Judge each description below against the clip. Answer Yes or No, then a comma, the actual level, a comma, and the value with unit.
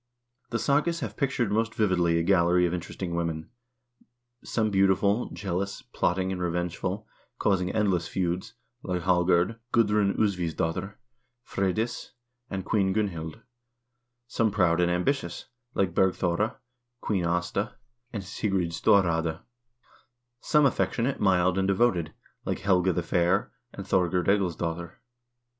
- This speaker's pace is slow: Yes, slow, 125 wpm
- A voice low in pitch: Yes, very low, 95 Hz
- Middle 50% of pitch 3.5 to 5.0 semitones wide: No, average, 3.0 semitones